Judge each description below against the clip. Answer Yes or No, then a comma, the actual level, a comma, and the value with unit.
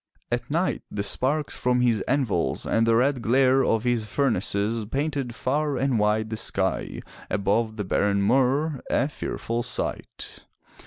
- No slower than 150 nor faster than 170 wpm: Yes, average, 155 wpm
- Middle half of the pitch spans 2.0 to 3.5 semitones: No, average, 3.9 semitones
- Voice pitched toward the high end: No, low, 120 Hz